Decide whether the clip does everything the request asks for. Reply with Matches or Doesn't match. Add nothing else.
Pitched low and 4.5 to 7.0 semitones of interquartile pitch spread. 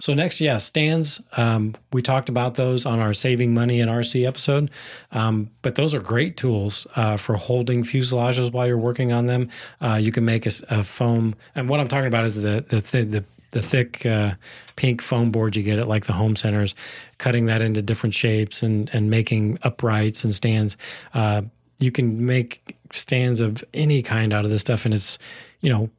Doesn't match